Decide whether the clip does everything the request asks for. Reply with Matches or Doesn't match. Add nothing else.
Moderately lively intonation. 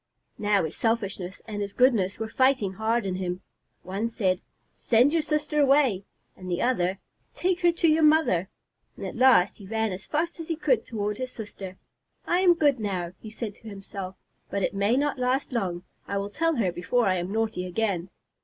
Doesn't match